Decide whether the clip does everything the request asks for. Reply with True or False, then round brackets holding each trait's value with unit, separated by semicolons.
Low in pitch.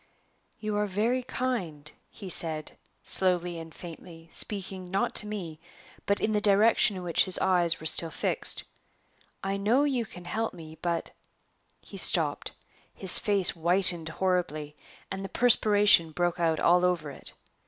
False (180 Hz)